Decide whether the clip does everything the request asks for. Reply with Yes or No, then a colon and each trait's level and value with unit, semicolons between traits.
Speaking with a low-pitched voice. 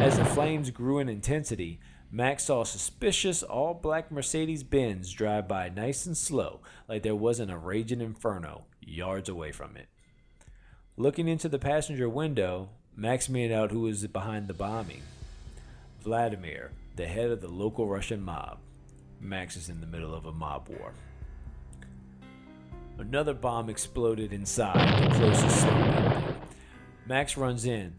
Yes: low, 110 Hz